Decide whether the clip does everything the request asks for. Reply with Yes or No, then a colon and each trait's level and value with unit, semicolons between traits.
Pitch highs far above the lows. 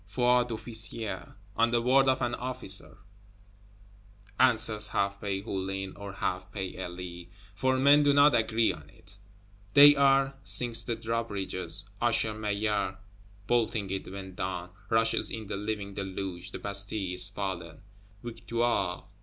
No: average, 3.7 semitones